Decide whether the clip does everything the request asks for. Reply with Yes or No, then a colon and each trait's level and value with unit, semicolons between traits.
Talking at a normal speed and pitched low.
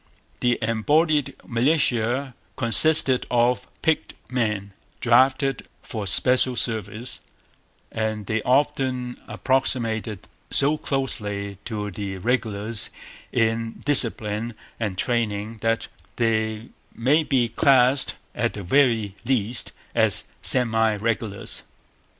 No: slow, 95 wpm; low, 115 Hz